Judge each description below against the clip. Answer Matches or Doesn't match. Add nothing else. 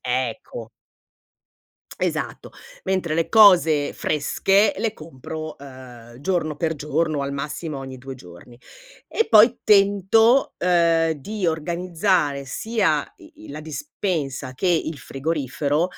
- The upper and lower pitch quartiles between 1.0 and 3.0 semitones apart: Doesn't match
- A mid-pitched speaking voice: Matches